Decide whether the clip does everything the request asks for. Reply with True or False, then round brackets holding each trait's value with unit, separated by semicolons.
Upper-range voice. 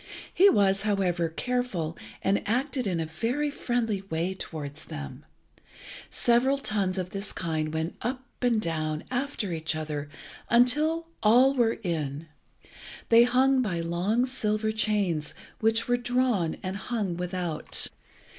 True (205 Hz)